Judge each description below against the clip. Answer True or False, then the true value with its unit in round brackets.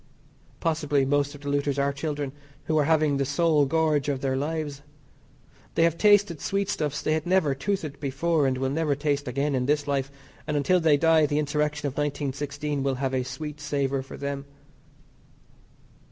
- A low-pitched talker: False (145 Hz)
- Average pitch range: False (2.0 semitones)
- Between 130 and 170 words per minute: False (180 wpm)